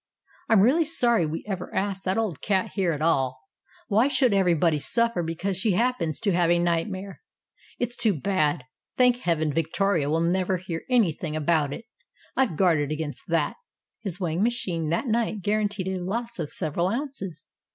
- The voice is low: No, medium, 185 Hz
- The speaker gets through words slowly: No, average, 170 wpm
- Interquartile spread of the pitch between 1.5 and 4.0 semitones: No, average, 4.8 semitones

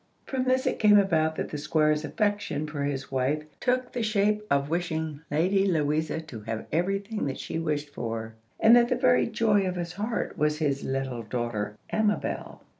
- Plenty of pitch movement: Yes, wide, 6.5 semitones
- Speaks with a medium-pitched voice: Yes, medium, 160 Hz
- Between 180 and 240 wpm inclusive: Yes, average, 190 wpm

